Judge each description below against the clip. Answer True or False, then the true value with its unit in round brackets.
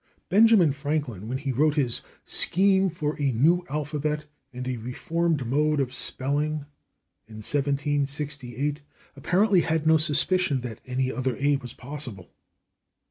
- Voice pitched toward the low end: False (145 Hz)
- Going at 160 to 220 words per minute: False (135 wpm)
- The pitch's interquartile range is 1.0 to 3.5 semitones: True (3.2 semitones)